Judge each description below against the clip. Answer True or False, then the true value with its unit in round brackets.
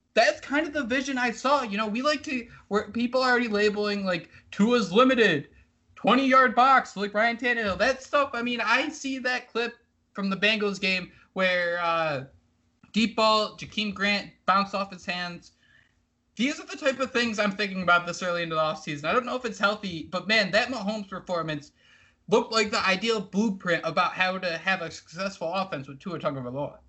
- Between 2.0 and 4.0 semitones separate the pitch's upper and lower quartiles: False (5.0 semitones)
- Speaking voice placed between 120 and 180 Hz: False (210 Hz)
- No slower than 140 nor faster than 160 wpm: False (195 wpm)